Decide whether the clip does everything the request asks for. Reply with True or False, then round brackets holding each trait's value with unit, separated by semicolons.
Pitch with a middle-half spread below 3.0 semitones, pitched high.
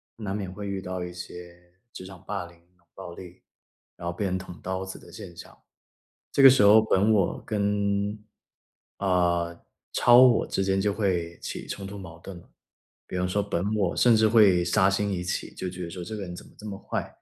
False (2.5 semitones; 95 Hz)